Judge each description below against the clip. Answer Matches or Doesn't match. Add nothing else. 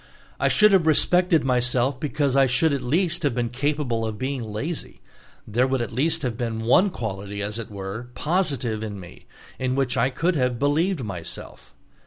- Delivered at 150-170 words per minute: Doesn't match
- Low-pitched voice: Matches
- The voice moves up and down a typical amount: Matches